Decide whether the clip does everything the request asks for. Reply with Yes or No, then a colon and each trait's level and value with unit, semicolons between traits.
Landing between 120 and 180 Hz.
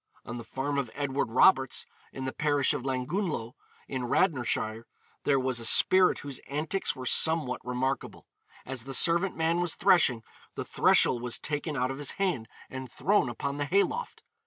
Yes: low, 135 Hz